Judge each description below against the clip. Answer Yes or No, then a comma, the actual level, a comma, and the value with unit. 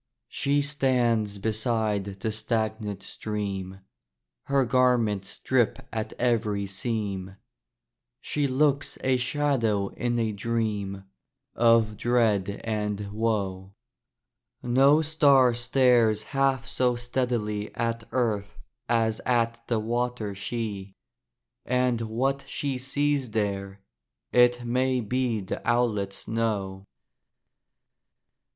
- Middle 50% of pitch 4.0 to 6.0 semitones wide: No, average, 3.3 semitones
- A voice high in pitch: No, low, 115 Hz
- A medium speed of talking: No, slow, 100 wpm